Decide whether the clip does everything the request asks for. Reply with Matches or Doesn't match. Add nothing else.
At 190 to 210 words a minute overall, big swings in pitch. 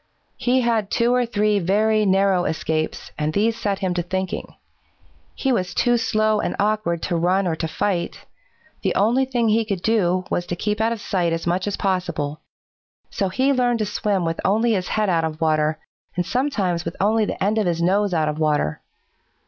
Doesn't match